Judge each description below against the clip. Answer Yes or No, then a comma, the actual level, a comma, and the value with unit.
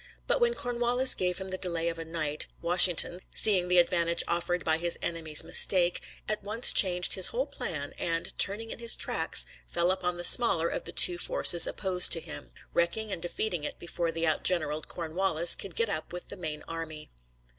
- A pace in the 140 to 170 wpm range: No, average, 190 wpm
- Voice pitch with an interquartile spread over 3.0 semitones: No, average, 2.7 semitones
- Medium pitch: Yes, medium, 175 Hz